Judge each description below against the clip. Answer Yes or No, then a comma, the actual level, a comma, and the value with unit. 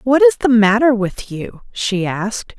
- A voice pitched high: Yes, high, 220 Hz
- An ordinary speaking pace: Yes, average, 185 wpm